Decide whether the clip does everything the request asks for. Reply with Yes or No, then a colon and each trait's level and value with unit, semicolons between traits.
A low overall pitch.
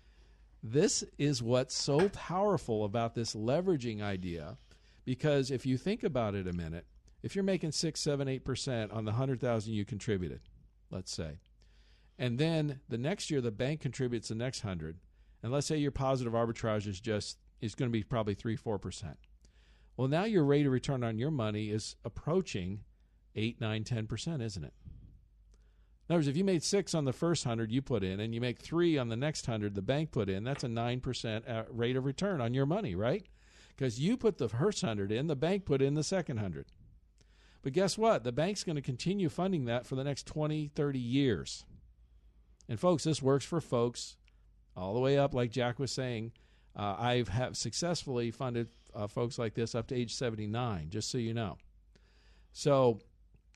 Yes: low, 120 Hz